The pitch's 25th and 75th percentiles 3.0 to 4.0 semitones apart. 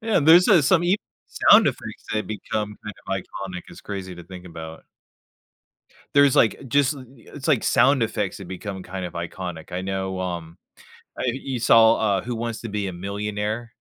No: average, 4.5 semitones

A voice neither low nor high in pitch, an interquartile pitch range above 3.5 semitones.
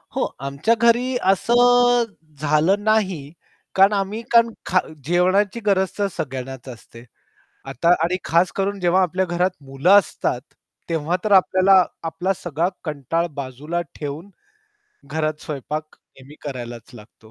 Yes: medium, 175 Hz; average, 5.3 semitones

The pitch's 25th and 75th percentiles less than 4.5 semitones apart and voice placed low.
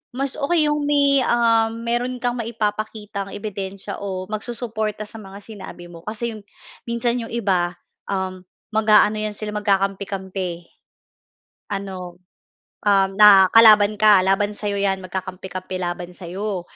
No: average, 2.9 semitones; high, 205 Hz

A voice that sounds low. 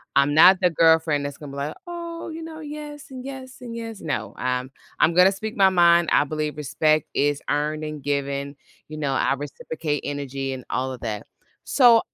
No: medium, 155 Hz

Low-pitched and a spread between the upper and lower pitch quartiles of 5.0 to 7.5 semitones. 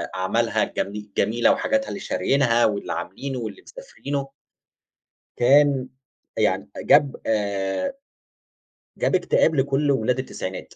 Yes: low, 130 Hz; average, 5.3 semitones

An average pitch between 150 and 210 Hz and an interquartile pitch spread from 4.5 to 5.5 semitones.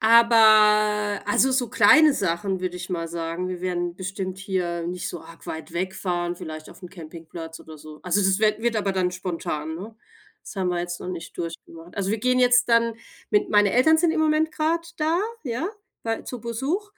Yes: high, 190 Hz; average, 4.9 semitones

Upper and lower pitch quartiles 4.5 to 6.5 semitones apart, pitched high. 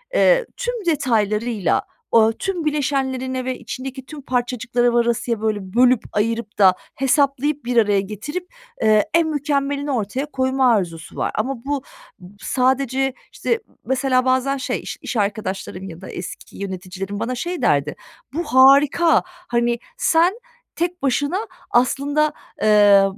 Yes: average, 4.8 semitones; very high, 255 Hz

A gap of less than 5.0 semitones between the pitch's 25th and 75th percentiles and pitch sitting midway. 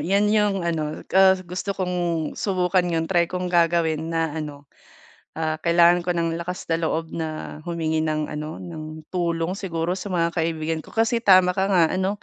Yes: narrow, 2.4 semitones; medium, 170 Hz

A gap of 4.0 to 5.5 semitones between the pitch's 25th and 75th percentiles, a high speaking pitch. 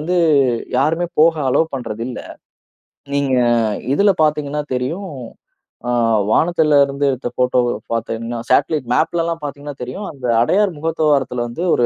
No: average, 4.3 semitones; medium, 145 Hz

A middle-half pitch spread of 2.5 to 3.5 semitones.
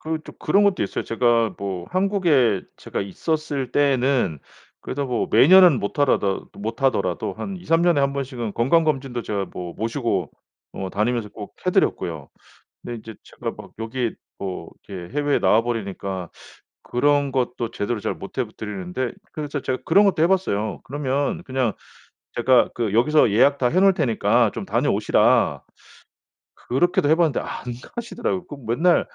No: wide, 5.5 semitones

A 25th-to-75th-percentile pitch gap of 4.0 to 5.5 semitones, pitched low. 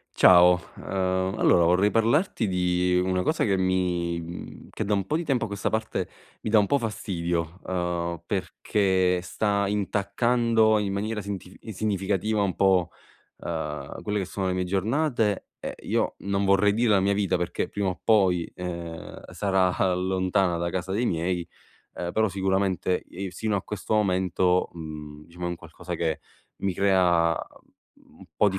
No: narrow, 2.6 semitones; very low, 95 Hz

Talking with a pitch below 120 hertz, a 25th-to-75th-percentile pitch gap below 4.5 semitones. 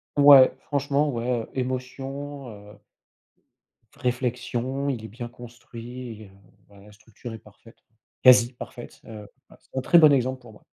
No: low, 125 Hz; average, 2.8 semitones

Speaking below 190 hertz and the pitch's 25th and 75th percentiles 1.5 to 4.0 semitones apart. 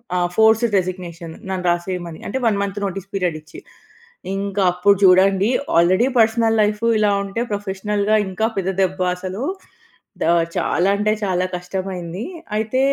No: high, 195 Hz; narrow, 2.4 semitones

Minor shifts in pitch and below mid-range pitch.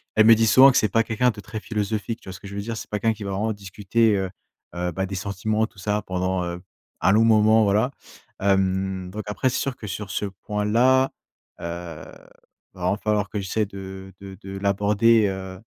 Yes: narrow, 2.3 semitones; low, 100 Hz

